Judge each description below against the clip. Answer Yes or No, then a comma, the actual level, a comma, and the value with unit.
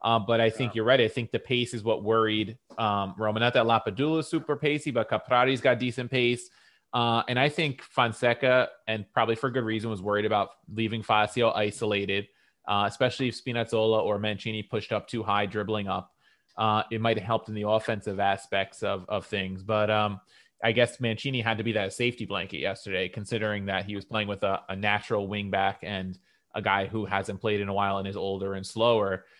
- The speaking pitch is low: Yes, low, 110 Hz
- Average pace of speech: No, fast, 210 wpm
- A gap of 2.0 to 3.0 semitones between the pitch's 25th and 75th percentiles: Yes, narrow, 2.5 semitones